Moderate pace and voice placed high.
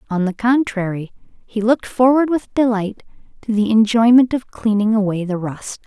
Yes: average, 165 wpm; high, 220 Hz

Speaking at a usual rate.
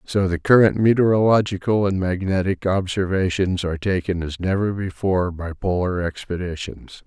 No: slow, 125 wpm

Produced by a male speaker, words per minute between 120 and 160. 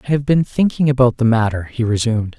No: male; fast, 225 wpm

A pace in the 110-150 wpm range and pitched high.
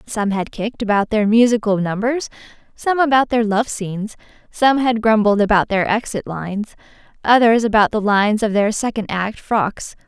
No: average, 165 wpm; high, 215 Hz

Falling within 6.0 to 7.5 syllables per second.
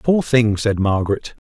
No: 4.7 syllables/s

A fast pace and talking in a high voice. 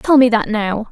Yes: fast, 260 wpm; high, 230 Hz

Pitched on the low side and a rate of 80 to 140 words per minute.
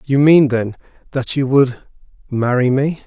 Yes: low, 130 Hz; slow, 135 wpm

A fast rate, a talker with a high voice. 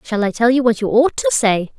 Yes: fast, 305 wpm; high, 240 Hz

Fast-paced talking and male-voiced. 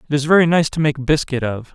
Yes: fast, 275 wpm; male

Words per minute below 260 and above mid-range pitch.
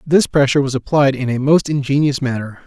No: average, 200 wpm; low, 135 Hz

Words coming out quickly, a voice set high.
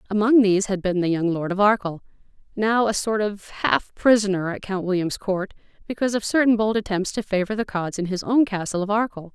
Yes: fast, 220 wpm; high, 200 Hz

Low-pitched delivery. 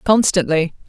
No: medium, 175 Hz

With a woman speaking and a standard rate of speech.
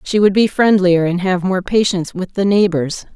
No: female; fast, 210 wpm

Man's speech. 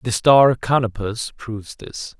Yes: male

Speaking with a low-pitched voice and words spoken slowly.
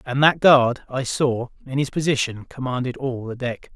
No: low, 130 Hz; average, 190 wpm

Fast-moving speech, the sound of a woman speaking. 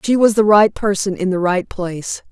Yes: fast, 235 wpm; female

